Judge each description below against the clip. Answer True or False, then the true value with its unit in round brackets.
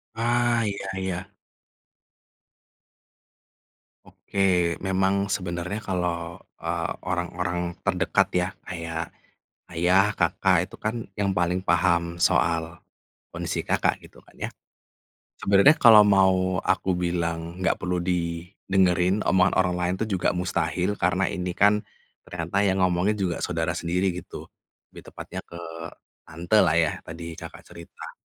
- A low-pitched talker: True (90 Hz)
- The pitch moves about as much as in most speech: False (2.0 semitones)